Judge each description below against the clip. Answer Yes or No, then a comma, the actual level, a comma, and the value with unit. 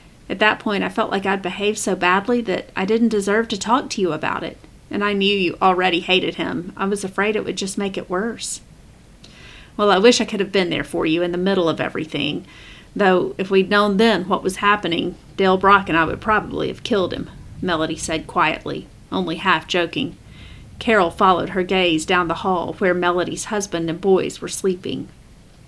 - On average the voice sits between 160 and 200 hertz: Yes, high, 190 Hz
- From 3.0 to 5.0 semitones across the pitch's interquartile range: No, narrow, 2.6 semitones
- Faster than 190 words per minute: Yes, fast, 205 wpm